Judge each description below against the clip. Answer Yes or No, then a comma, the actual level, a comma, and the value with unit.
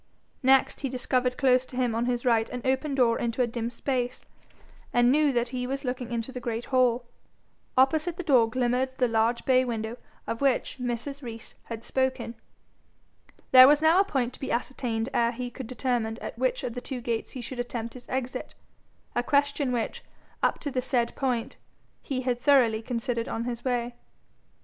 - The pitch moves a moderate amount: No, narrow, 1.9 semitones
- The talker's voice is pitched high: Yes, very high, 250 Hz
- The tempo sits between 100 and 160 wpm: No, average, 190 wpm